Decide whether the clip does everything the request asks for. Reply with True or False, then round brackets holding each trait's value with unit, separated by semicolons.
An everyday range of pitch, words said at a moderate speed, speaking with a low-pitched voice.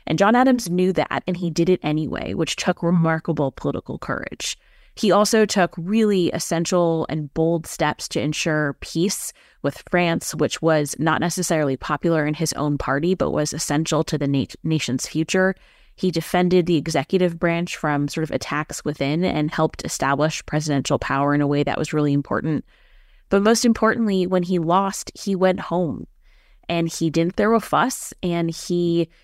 False (3.3 semitones; 170 wpm; 165 Hz)